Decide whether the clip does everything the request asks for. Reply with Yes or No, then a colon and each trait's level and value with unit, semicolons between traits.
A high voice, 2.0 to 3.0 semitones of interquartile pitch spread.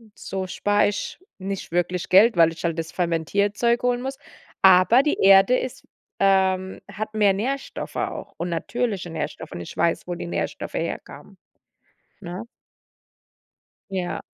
No: high, 195 Hz; average, 3.4 semitones